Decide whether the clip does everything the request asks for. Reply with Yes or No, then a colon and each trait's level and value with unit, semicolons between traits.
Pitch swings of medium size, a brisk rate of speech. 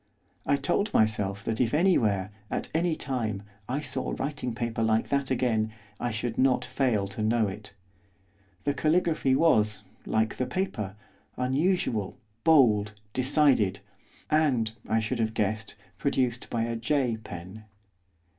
No: average, 4.4 semitones; slow, 135 wpm